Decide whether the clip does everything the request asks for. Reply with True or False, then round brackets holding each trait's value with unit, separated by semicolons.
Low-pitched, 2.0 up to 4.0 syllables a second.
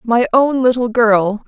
False (235 Hz; 3.9 syllables/s)